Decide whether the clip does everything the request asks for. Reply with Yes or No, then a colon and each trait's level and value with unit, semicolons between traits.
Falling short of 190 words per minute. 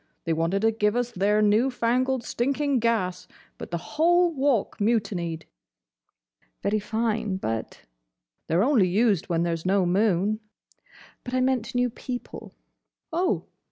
Yes: average, 140 wpm